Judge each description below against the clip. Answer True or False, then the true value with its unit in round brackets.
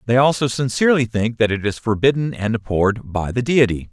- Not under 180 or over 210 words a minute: True (200 wpm)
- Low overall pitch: True (120 Hz)